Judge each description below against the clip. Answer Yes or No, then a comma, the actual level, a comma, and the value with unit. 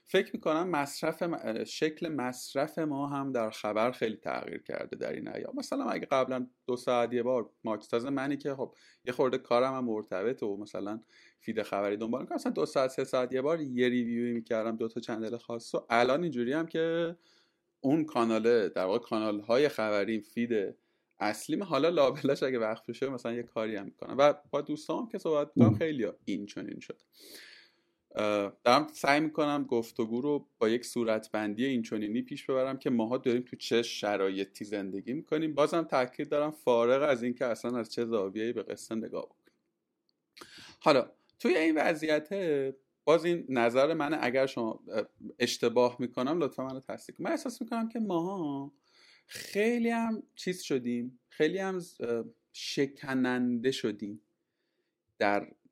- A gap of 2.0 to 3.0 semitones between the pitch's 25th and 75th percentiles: No, average, 4.4 semitones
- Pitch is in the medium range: No, low, 125 Hz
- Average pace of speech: No, fast, 160 wpm